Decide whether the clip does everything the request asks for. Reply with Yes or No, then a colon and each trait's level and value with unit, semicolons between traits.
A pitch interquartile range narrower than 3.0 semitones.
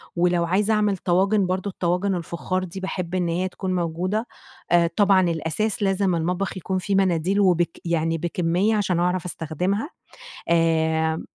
Yes: narrow, 2.4 semitones